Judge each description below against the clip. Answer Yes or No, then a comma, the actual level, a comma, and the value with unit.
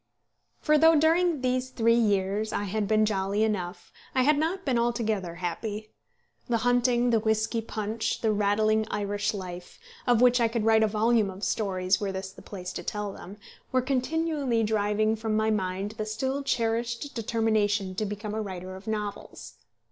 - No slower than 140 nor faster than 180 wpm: Yes, average, 175 wpm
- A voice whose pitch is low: No, high, 220 Hz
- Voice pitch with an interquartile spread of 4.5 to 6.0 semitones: No, average, 2.7 semitones